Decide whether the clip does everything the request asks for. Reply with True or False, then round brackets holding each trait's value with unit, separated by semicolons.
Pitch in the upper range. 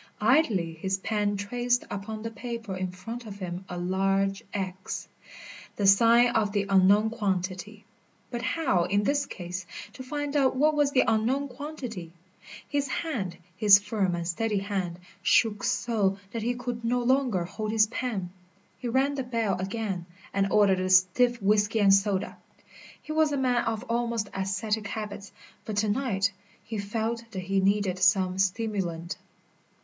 True (210 Hz)